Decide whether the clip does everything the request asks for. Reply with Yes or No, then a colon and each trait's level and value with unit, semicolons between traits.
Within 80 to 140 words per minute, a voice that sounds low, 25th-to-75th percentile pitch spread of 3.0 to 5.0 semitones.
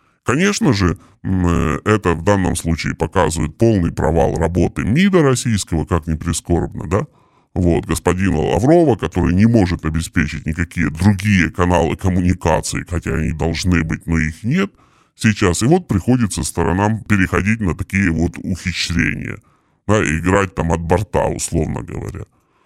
Yes: average, 135 wpm; very low, 90 Hz; average, 4.0 semitones